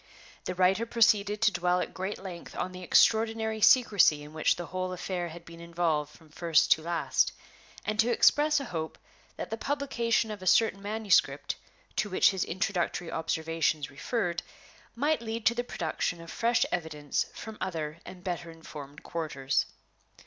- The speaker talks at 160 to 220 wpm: Yes, average, 165 wpm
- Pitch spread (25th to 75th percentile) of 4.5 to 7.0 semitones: Yes, average, 5.1 semitones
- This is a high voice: No, medium, 180 Hz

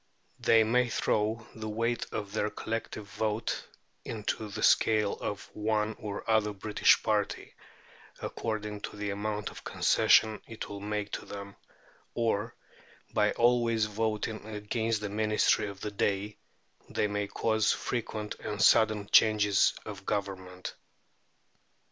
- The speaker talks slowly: Yes, slow, 130 wpm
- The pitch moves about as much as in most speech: No, narrow, 1.3 semitones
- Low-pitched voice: Yes, low, 105 Hz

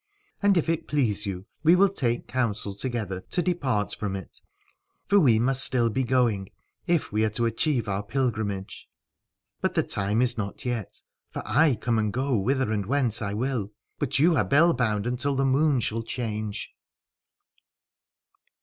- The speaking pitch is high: No, low, 120 Hz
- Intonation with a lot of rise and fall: No, average, 4.5 semitones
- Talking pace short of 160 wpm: No, average, 170 wpm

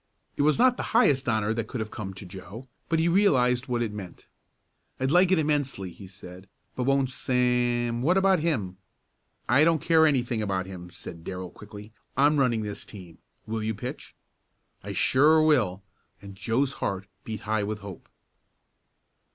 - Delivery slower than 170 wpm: No, average, 175 wpm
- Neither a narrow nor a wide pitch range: No, wide, 6.0 semitones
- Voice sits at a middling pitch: No, low, 120 Hz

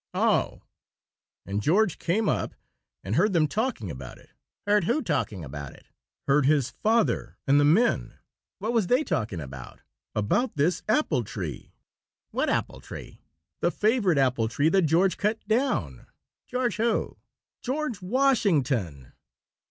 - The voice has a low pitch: No, medium, 165 Hz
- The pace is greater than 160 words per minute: No, average, 145 wpm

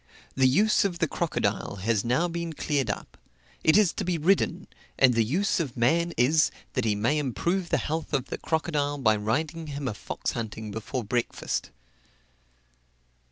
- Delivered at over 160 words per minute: Yes, average, 170 wpm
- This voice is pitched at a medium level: Yes, medium, 145 Hz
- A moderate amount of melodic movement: No, wide, 6.2 semitones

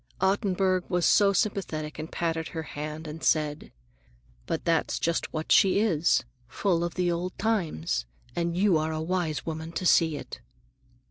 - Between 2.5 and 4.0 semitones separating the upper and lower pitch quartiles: Yes, average, 2.9 semitones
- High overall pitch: No, medium, 170 Hz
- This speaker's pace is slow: No, average, 160 wpm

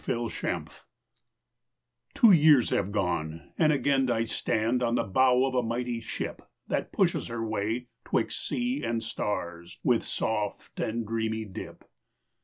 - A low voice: Yes, low, 115 Hz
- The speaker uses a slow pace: No, average, 145 wpm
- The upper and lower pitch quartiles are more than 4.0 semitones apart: No, average, 2.8 semitones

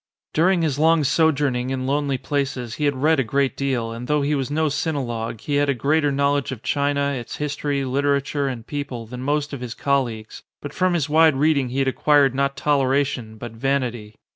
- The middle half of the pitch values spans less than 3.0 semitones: Yes, narrow, 2.4 semitones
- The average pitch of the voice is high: No, medium, 140 Hz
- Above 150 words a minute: Yes, average, 200 wpm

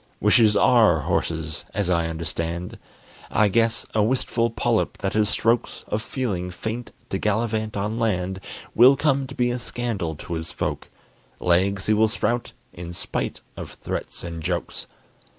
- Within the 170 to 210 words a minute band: No, average, 155 wpm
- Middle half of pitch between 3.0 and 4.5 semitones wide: No, average, 4.9 semitones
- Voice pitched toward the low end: Yes, low, 105 Hz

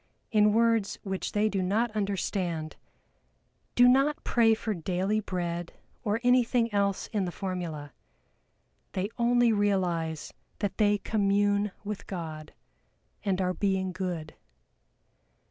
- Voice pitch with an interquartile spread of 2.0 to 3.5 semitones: Yes, average, 2.9 semitones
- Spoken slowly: Yes, slow, 120 wpm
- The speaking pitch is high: Yes, high, 200 Hz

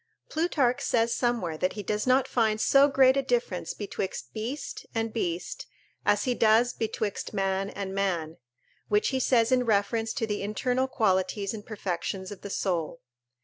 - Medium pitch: No, high, 215 Hz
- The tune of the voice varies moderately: Yes, average, 4.0 semitones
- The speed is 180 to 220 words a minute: No, average, 165 wpm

